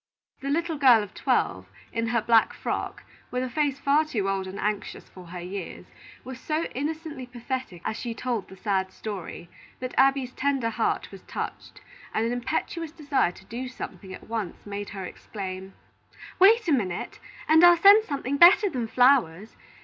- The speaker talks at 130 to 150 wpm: No, average, 175 wpm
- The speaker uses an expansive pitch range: Yes, wide, 5.9 semitones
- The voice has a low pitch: No, high, 245 Hz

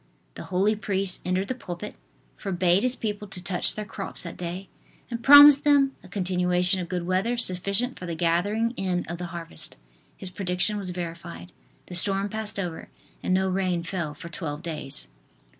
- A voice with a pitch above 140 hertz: Yes, medium, 185 Hz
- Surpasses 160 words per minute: Yes, average, 175 wpm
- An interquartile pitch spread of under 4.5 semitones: Yes, average, 2.8 semitones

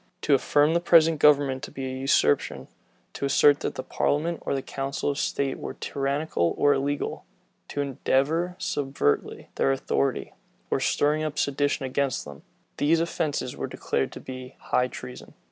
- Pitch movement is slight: Yes, narrow, 2.1 semitones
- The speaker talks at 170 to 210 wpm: No, average, 160 wpm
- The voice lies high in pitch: No, medium, 140 Hz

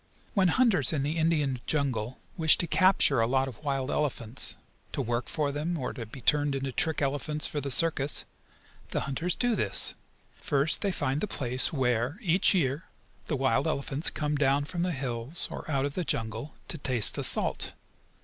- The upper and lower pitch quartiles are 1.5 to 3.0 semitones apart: No, average, 3.4 semitones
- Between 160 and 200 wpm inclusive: Yes, average, 190 wpm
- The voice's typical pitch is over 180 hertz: No, medium, 145 Hz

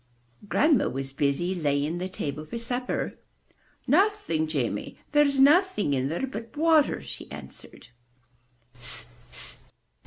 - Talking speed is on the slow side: Yes, slow, 115 wpm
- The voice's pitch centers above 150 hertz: Yes, medium, 185 Hz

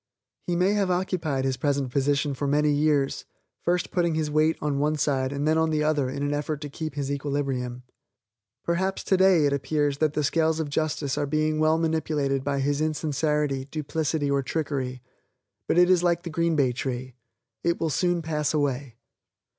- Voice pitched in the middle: Yes, medium, 150 Hz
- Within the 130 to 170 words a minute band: No, average, 185 wpm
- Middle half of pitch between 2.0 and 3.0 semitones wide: Yes, narrow, 2.4 semitones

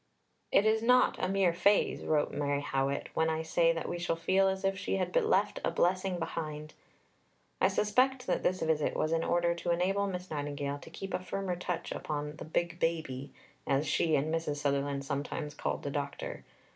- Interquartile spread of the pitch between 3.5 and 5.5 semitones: Yes, average, 4.0 semitones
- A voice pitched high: No, medium, 165 Hz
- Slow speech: No, average, 195 wpm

